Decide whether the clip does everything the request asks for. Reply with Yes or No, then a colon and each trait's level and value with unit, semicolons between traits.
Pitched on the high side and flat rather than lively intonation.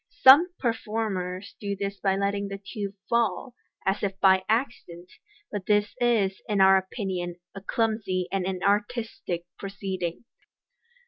Yes: high, 200 Hz; narrow, 2.2 semitones